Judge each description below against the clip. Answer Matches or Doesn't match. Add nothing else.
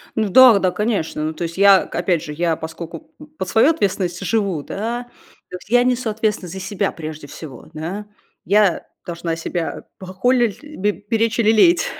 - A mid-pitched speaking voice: Doesn't match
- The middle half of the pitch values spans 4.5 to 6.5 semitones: Matches